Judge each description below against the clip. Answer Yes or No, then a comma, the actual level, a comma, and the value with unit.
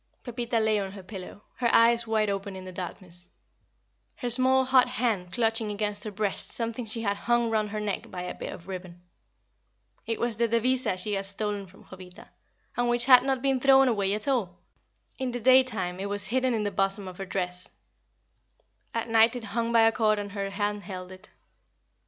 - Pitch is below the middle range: No, high, 215 Hz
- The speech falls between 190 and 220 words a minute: Yes, average, 200 wpm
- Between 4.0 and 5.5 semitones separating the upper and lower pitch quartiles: No, average, 3.4 semitones